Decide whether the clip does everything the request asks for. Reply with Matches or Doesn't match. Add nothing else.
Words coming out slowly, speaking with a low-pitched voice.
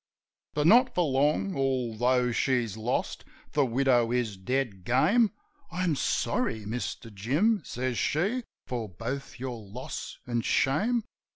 Matches